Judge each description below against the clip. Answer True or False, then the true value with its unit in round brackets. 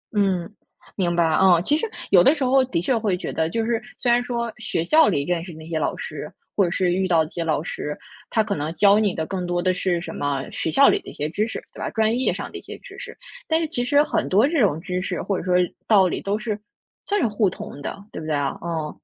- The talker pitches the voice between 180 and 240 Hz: True (190 Hz)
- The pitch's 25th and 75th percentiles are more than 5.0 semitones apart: True (5.5 semitones)